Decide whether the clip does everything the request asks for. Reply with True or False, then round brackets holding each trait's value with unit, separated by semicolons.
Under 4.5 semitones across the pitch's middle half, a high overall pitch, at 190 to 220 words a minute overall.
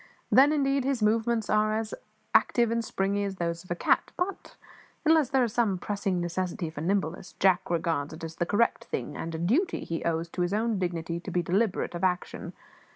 False (5.0 semitones; 195 Hz; 205 wpm)